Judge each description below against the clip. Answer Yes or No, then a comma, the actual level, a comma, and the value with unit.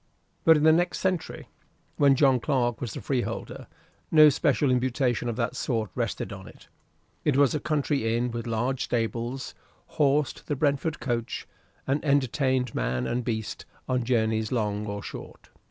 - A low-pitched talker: Yes, low, 125 Hz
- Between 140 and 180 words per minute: Yes, average, 160 wpm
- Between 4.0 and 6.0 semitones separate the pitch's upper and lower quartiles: No, average, 3.5 semitones